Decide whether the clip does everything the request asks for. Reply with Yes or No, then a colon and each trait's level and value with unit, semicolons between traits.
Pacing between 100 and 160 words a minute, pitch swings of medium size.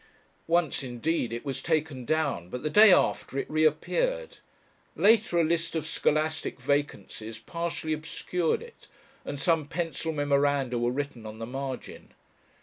Yes: average, 145 wpm; average, 3.7 semitones